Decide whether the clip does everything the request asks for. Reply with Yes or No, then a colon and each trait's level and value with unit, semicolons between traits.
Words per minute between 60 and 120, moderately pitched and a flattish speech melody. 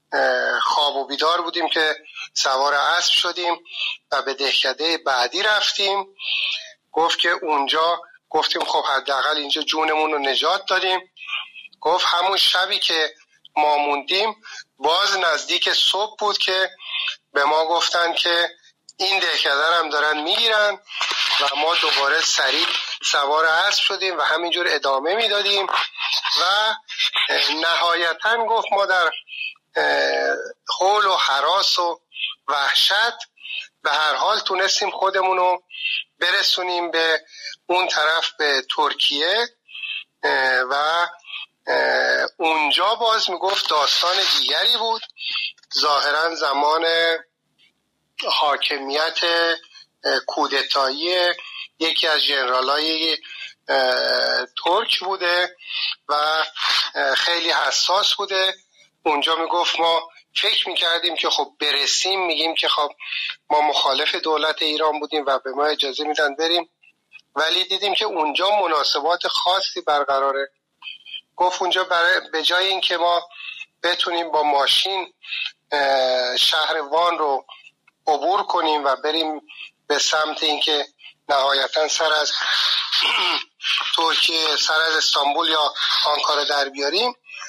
No: average, 110 wpm; medium, 165 Hz; average, 3.4 semitones